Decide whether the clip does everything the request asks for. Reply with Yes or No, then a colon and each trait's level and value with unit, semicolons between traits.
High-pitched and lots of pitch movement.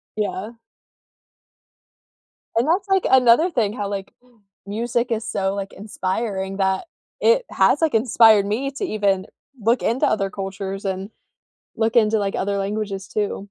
No: high, 210 Hz; average, 3.2 semitones